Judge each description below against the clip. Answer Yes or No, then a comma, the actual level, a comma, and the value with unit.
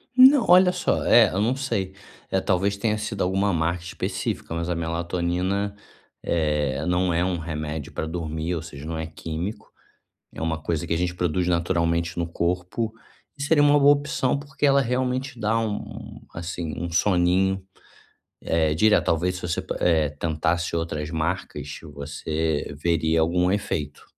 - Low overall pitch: Yes, very low, 90 Hz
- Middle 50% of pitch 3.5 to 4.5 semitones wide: Yes, average, 3.9 semitones